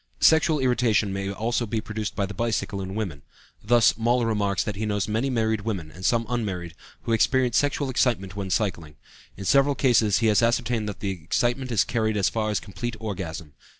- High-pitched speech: No, low, 110 Hz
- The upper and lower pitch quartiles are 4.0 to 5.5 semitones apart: No, average, 3.4 semitones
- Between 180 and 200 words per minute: Yes, average, 195 wpm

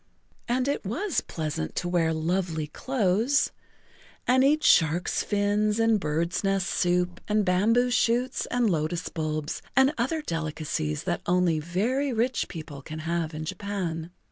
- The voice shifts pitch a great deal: Yes, wide, 6.3 semitones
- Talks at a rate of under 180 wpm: Yes, average, 145 wpm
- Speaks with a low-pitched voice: No, medium, 180 Hz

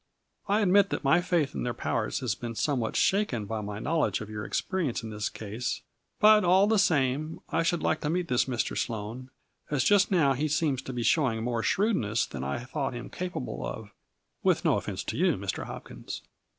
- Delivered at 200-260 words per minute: Yes, fast, 205 wpm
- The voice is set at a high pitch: No, low, 135 Hz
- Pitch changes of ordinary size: No, wide, 7.4 semitones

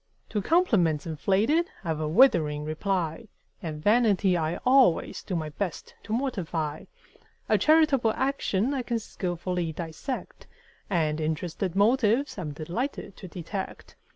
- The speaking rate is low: Yes, slow, 125 wpm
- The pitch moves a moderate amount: No, wide, 6.9 semitones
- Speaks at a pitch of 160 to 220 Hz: Yes, medium, 185 Hz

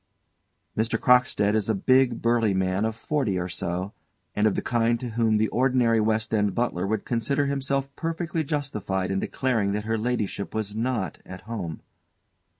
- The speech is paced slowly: No, average, 175 wpm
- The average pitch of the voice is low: Yes, low, 110 Hz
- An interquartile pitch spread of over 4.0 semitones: No, average, 3.5 semitones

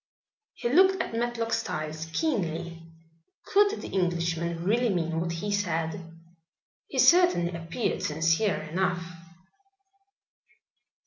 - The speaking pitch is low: No, medium, 175 Hz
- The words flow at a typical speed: No, slow, 105 wpm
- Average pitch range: No, wide, 5.7 semitones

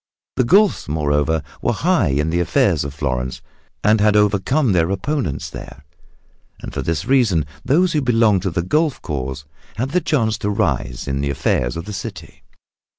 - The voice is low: Yes, very low, 95 Hz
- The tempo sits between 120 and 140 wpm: No, average, 175 wpm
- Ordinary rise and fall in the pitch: No, wide, 8.9 semitones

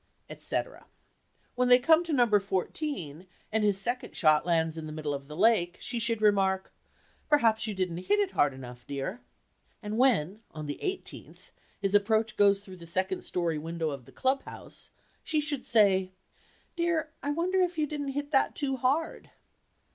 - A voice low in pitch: No, high, 210 Hz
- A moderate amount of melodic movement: No, wide, 8.0 semitones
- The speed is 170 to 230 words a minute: Yes, average, 180 wpm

